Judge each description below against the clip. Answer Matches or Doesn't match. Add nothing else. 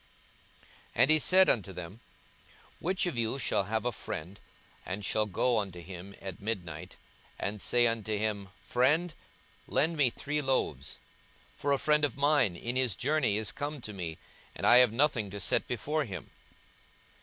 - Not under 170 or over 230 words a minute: Matches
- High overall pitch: Doesn't match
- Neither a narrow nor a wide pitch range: Doesn't match